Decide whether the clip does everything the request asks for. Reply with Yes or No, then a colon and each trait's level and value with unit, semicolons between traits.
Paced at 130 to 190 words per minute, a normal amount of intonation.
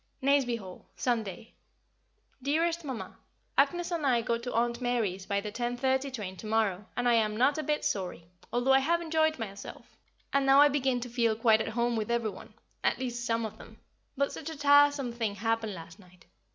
No: average, 200 wpm; average, 4.0 semitones